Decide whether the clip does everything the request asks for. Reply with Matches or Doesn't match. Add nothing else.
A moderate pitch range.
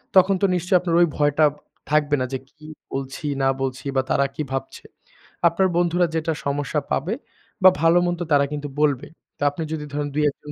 Matches